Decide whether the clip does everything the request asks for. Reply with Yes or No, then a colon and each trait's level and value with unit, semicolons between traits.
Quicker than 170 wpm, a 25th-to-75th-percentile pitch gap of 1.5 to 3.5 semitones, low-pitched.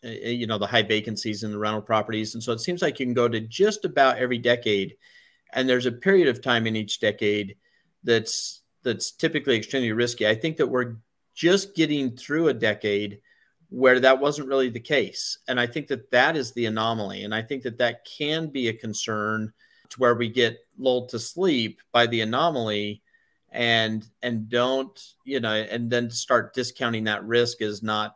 Yes: average, 195 wpm; average, 3.0 semitones; low, 120 Hz